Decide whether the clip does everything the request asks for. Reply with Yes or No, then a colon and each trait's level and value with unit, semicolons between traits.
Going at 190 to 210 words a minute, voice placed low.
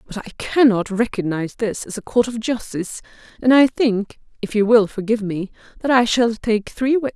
No: average, 200 wpm; high, 225 Hz